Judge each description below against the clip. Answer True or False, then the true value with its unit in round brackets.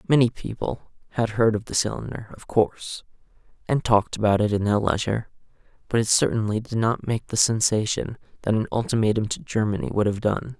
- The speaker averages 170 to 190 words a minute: True (180 wpm)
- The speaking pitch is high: False (110 Hz)